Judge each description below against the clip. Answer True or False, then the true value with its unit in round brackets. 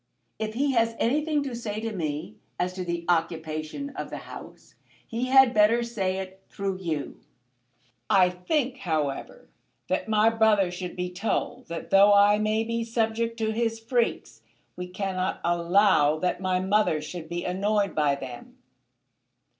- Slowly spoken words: False (155 wpm)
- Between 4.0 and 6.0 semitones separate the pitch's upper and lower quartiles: True (4.3 semitones)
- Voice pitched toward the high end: True (200 Hz)